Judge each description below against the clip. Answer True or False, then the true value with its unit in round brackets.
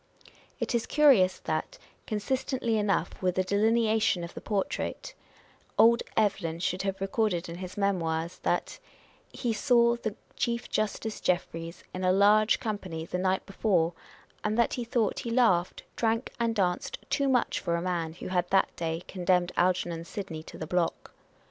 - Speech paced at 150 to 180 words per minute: True (165 wpm)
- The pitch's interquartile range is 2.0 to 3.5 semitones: False (4.2 semitones)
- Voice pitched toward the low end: False (195 Hz)